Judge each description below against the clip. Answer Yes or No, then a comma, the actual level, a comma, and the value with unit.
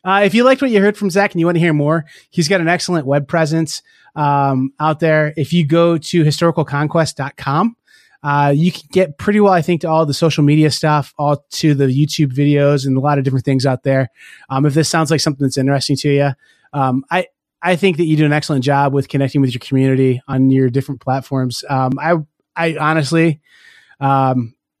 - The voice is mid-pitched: Yes, medium, 150 Hz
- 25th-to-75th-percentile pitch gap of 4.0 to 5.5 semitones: No, average, 3.3 semitones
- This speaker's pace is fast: Yes, fast, 220 wpm